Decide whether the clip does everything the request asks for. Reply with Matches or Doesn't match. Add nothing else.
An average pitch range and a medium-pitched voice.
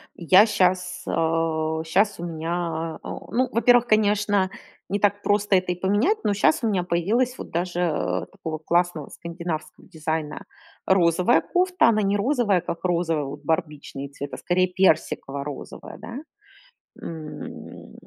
Matches